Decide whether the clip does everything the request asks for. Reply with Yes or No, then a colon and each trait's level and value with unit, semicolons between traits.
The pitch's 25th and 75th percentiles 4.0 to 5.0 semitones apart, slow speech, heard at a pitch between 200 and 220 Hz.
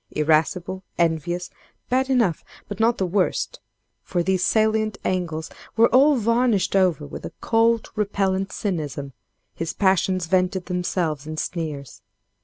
No: average, 4.6 semitones; slow, 125 wpm; medium, 185 Hz